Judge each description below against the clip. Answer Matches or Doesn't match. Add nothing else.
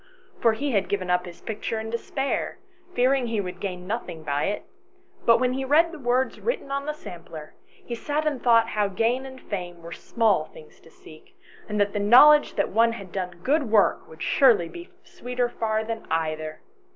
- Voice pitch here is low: Doesn't match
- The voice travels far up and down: Matches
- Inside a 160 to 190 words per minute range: Doesn't match